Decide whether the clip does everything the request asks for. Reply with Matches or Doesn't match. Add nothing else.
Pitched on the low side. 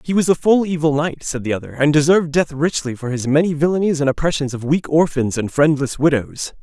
Doesn't match